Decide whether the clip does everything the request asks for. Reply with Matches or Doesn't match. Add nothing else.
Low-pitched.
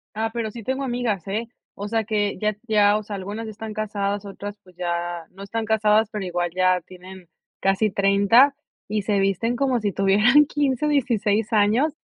Doesn't match